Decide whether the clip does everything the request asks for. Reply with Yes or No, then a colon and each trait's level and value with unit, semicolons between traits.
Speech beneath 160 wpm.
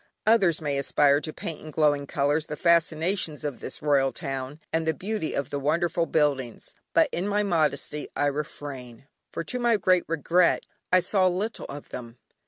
No: average, 180 wpm